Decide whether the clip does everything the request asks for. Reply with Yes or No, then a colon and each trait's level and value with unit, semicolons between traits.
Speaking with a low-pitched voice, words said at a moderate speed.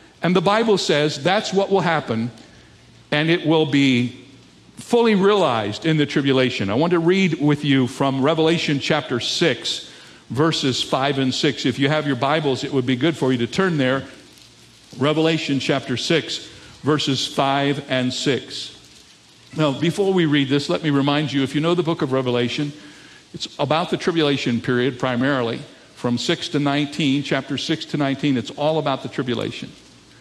No: medium, 145 Hz; average, 175 wpm